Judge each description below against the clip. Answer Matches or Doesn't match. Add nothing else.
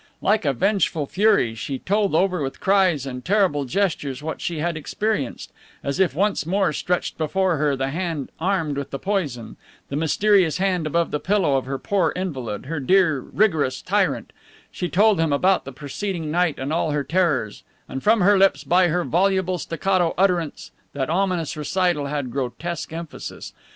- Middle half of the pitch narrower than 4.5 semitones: Doesn't match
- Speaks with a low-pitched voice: Doesn't match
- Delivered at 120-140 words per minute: Doesn't match